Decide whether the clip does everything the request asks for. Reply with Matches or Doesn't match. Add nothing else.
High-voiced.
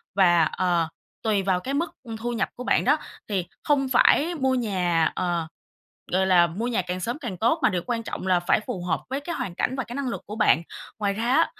Matches